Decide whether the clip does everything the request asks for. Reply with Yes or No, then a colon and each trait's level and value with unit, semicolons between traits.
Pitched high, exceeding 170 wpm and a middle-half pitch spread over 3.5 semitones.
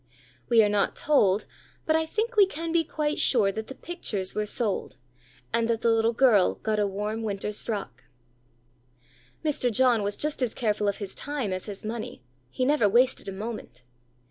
Yes: high, 225 Hz; average, 185 wpm; average, 4.5 semitones